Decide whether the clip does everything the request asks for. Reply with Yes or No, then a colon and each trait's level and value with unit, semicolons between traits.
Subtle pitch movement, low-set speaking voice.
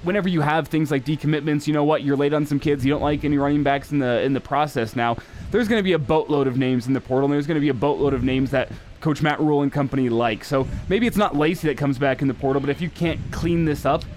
No: narrow, 2.2 semitones; medium, 145 Hz